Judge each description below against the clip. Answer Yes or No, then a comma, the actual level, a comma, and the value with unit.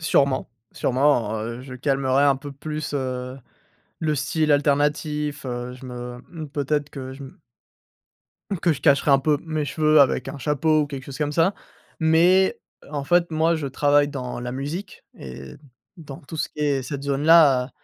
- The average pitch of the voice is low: No, medium, 145 Hz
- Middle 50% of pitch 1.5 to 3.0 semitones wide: Yes, narrow, 2.6 semitones